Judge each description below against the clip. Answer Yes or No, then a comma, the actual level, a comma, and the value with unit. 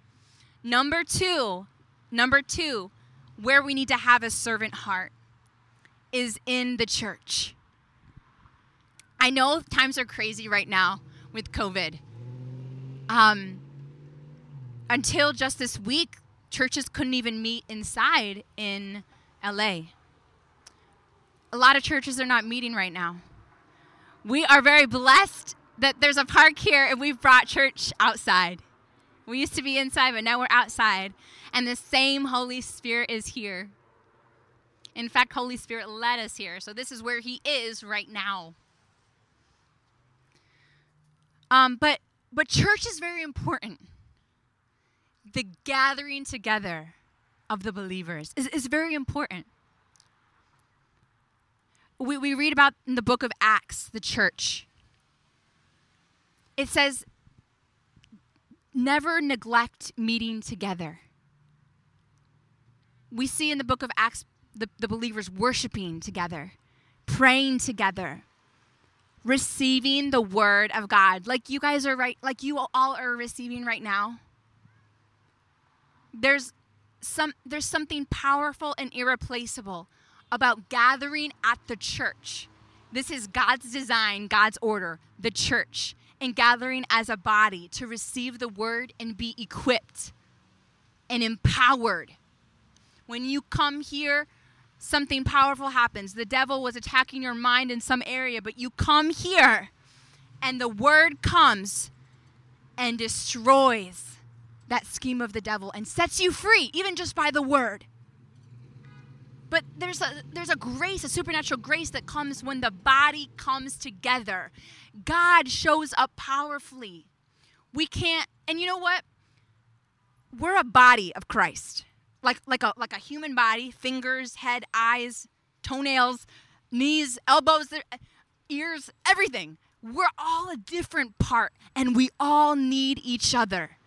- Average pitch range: No, wide, 8.6 semitones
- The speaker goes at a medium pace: No, slow, 130 wpm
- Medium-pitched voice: No, high, 235 Hz